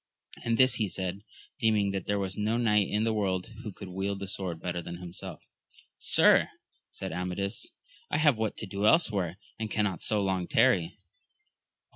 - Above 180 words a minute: No, average, 175 wpm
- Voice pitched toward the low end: Yes, low, 100 Hz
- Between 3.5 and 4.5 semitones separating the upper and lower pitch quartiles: No, average, 2.9 semitones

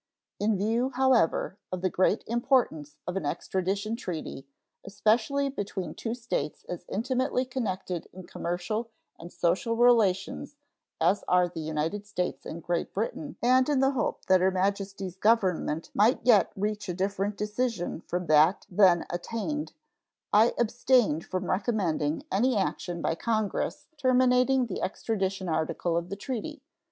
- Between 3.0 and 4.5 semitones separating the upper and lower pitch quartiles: No, average, 5.0 semitones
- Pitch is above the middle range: Yes, high, 200 Hz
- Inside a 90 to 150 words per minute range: Yes, average, 145 wpm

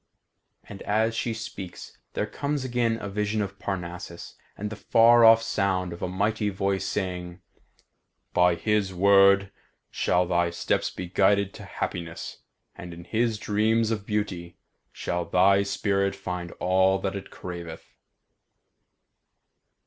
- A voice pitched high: No, low, 100 Hz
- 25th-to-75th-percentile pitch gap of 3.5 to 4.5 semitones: No, average, 2.8 semitones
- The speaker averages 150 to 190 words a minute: No, slow, 135 wpm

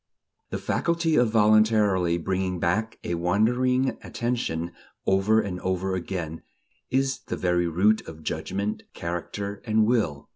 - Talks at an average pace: No, slow, 130 wpm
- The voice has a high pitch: No, low, 100 Hz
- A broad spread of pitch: No, average, 4.1 semitones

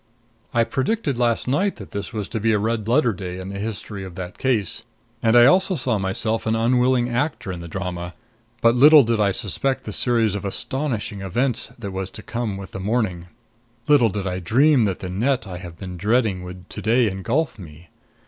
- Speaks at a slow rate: No, fast, 205 wpm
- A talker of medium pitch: No, low, 110 Hz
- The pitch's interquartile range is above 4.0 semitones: Yes, average, 4.5 semitones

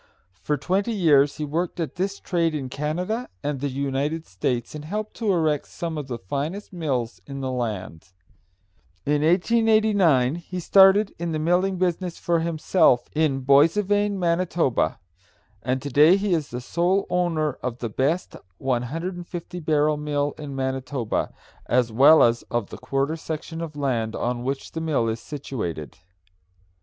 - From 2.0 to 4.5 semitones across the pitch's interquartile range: No, average, 4.9 semitones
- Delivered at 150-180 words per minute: Yes, average, 155 wpm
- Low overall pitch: No, medium, 150 Hz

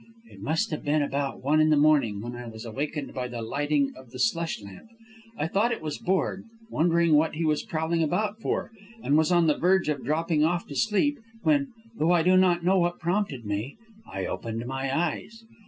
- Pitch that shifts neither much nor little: Yes, average, 4.2 semitones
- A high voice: No, medium, 155 Hz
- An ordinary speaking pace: No, fast, 210 wpm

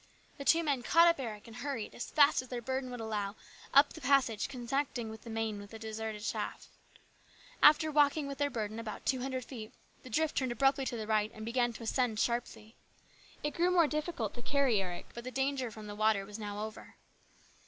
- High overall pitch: Yes, high, 240 Hz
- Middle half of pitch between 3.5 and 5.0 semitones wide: Yes, average, 4.2 semitones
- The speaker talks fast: Yes, fast, 210 wpm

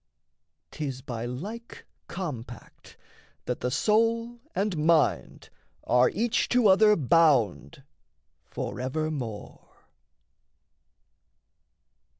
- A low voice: No, medium, 155 Hz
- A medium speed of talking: No, slow, 75 wpm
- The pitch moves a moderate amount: No, wide, 9.0 semitones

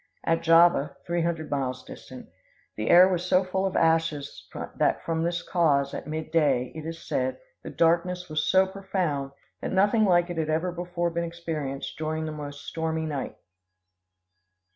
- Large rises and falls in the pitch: No, narrow, 2.4 semitones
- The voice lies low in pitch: No, medium, 165 Hz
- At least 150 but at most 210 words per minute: Yes, average, 170 wpm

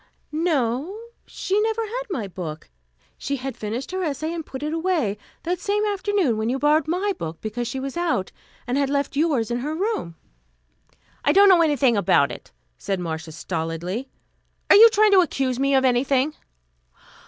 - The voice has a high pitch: Yes, very high, 280 Hz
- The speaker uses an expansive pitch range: Yes, wide, 7.3 semitones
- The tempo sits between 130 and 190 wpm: Yes, average, 175 wpm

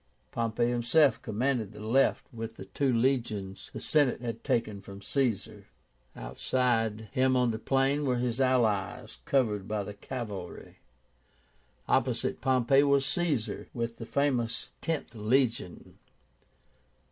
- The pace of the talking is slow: Yes, slow, 125 wpm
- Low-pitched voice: Yes, low, 120 Hz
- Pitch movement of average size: Yes, average, 3.5 semitones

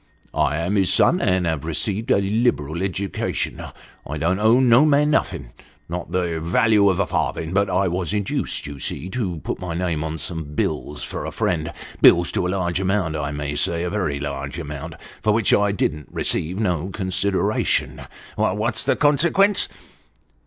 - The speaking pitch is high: No, very low, 90 Hz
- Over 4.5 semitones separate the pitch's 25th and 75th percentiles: No, average, 4.2 semitones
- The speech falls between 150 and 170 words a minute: No, average, 180 wpm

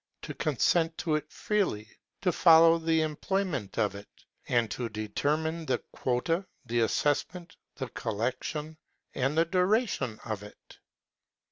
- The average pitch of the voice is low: No, medium, 155 Hz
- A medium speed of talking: No, slow, 130 wpm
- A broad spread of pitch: Yes, wide, 6.2 semitones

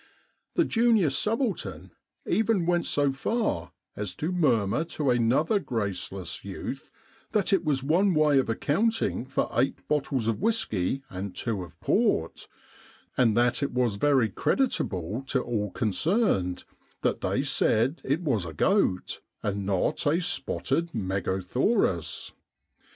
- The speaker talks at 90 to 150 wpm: Yes, average, 140 wpm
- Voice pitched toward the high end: No, low, 130 Hz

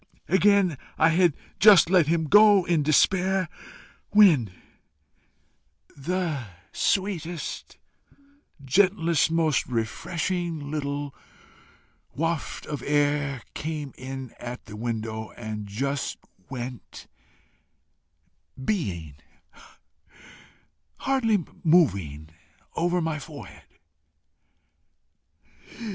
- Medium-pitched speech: Yes, medium, 155 Hz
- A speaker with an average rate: No, slow, 75 wpm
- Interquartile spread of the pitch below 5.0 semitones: No, wide, 5.5 semitones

